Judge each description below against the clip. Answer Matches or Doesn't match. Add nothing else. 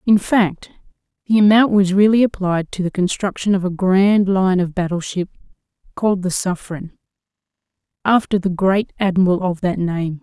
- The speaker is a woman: Matches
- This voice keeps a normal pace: Matches